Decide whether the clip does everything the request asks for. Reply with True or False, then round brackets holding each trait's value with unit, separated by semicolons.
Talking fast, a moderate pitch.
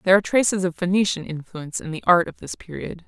True (235 wpm; 180 Hz)